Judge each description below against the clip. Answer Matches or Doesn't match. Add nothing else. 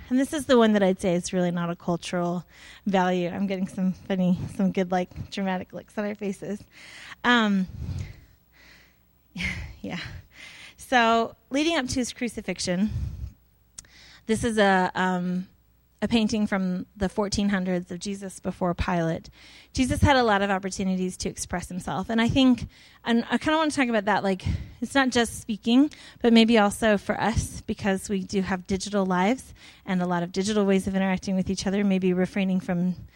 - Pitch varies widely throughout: Doesn't match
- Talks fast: Doesn't match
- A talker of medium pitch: Doesn't match